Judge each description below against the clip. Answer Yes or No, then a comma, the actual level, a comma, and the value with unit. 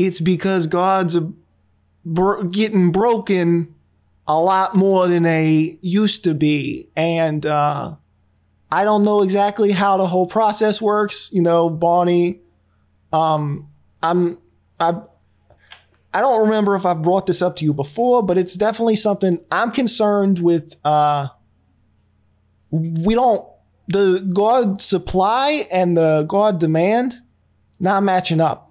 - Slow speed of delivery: Yes, slow, 130 wpm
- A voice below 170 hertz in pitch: No, medium, 175 Hz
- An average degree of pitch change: Yes, average, 4.3 semitones